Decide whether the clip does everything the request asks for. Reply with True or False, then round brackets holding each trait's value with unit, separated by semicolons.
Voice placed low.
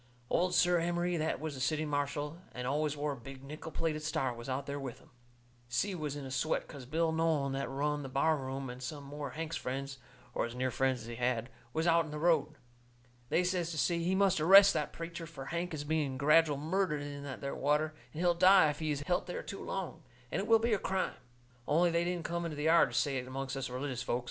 False (150 Hz)